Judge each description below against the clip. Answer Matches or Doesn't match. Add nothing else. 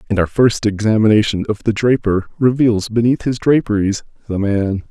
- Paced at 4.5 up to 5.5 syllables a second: Matches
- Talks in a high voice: Doesn't match